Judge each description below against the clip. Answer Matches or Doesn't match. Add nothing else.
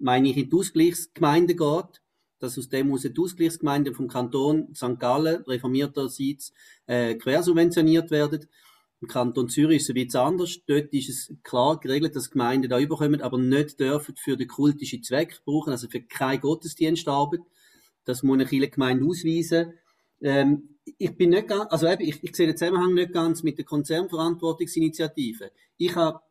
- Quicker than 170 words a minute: Doesn't match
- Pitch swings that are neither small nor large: Matches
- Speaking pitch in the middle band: Matches